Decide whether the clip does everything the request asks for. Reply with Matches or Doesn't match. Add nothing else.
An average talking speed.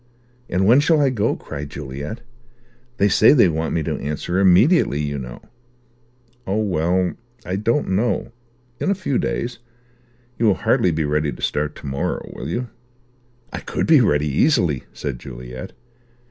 Matches